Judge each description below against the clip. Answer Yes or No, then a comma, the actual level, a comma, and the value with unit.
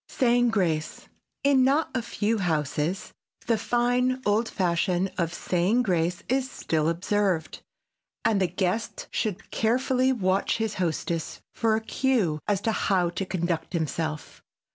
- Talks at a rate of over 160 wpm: No, average, 140 wpm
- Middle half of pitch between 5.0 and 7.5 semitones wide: Yes, wide, 5.5 semitones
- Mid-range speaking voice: No, high, 195 Hz